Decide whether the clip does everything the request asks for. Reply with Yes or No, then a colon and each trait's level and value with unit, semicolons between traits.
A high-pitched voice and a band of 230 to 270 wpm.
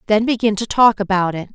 Yes: high, 210 Hz; fast, 235 wpm